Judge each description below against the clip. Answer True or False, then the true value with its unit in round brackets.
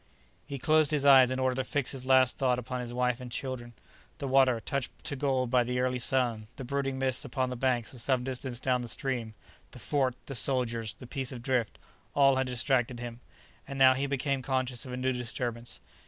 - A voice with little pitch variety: True (1.6 semitones)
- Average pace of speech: False (215 wpm)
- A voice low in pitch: True (130 Hz)